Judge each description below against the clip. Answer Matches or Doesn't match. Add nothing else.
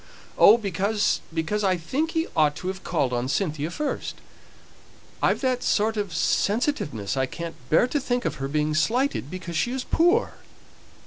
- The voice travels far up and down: Matches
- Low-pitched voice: Doesn't match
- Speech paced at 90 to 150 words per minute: Doesn't match